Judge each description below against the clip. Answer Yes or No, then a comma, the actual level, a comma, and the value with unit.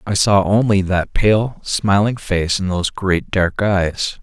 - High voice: No, low, 100 Hz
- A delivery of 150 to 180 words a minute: Yes, average, 170 wpm